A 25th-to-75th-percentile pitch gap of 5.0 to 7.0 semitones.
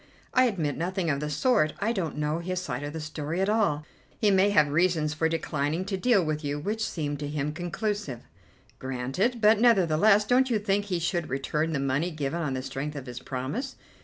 Yes: wide, 5.6 semitones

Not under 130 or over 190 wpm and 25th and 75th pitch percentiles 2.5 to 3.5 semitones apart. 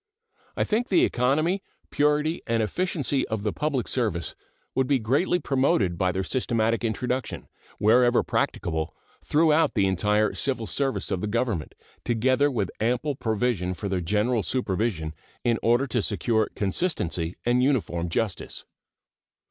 No: average, 140 wpm; average, 4.9 semitones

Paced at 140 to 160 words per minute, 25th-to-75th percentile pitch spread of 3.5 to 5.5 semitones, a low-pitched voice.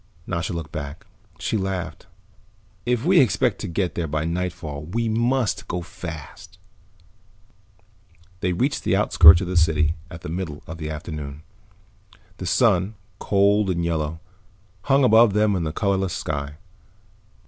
Yes: average, 150 wpm; average, 4.4 semitones; very low, 90 Hz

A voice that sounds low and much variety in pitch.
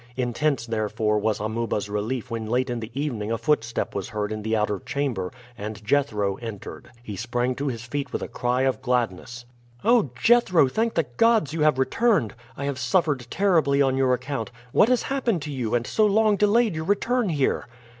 Yes: low, 130 Hz; wide, 5.8 semitones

